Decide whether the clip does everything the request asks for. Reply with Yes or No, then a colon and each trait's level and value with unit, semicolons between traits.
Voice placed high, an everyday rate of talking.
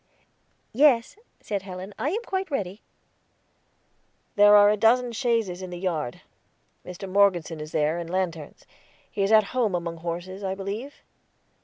Yes: high, 195 Hz; average, 150 wpm